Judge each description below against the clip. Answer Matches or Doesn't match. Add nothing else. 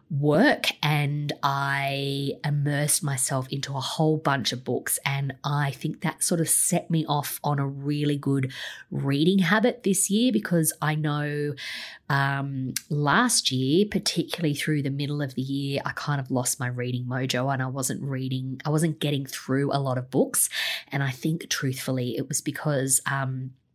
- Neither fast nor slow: Matches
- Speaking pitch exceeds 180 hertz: Doesn't match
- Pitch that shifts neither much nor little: Doesn't match